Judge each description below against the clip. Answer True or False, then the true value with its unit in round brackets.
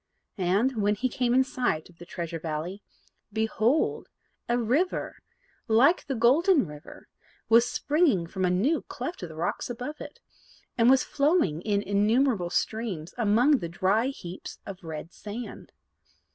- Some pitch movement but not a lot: False (6.2 semitones)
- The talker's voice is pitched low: False (220 Hz)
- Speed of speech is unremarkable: True (150 wpm)